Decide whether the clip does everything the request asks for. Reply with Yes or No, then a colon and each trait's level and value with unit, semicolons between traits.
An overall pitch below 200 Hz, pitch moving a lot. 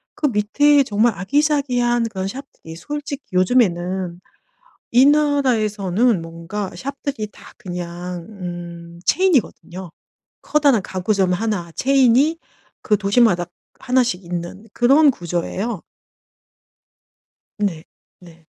No: high, 210 Hz; wide, 6.7 semitones